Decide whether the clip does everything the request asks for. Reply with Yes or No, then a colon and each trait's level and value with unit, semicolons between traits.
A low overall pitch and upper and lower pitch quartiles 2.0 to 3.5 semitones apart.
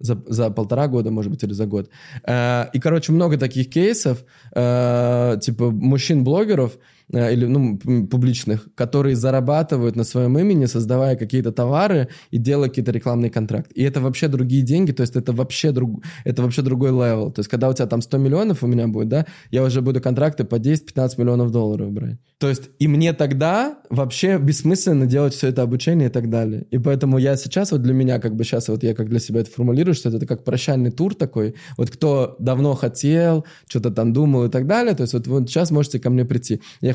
Yes: low, 130 Hz; average, 3.1 semitones